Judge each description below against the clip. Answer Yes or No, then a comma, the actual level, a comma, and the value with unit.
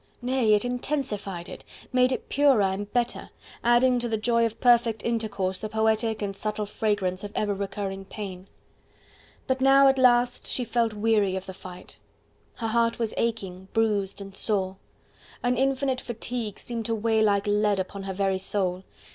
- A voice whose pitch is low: No, high, 220 Hz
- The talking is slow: No, average, 170 wpm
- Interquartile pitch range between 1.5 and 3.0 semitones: No, average, 3.4 semitones